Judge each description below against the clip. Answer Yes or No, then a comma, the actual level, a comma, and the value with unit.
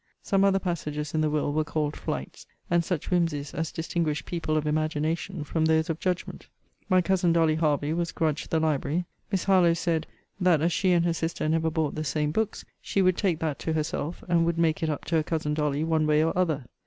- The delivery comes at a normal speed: No, fast, 220 wpm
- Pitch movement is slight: Yes, narrow, 2.0 semitones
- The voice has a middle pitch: Yes, medium, 160 Hz